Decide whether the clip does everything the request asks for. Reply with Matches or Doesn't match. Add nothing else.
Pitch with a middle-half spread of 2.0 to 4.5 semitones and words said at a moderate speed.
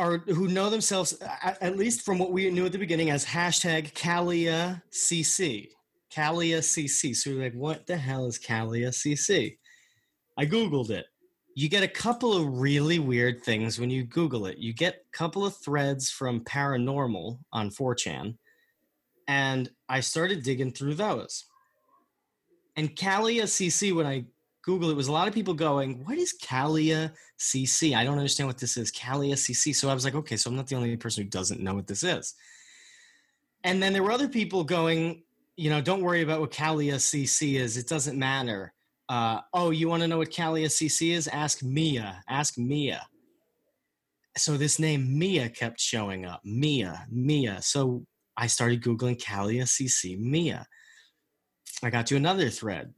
Doesn't match